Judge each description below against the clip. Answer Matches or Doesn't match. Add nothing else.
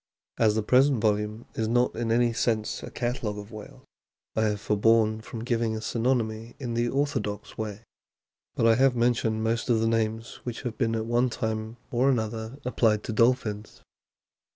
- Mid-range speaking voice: Doesn't match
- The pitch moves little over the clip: Matches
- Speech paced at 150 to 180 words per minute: Matches